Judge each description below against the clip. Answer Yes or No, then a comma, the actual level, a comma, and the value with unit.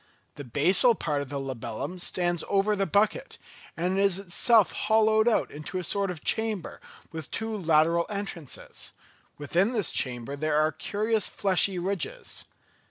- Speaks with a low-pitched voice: No, medium, 185 Hz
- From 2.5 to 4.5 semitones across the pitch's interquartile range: No, average, 5.3 semitones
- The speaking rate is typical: Yes, average, 150 wpm